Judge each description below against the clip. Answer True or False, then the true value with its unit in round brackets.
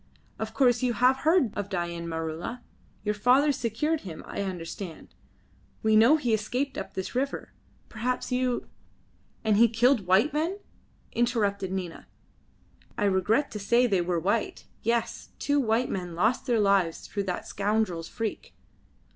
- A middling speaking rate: True (155 wpm)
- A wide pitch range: False (4.7 semitones)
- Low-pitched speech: False (220 Hz)